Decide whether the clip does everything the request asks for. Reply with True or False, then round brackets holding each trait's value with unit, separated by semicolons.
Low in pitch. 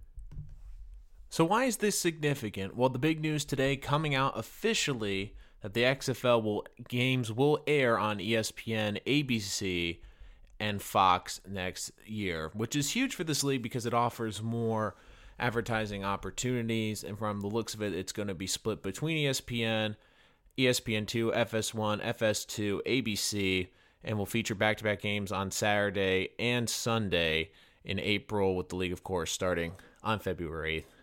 True (110 Hz)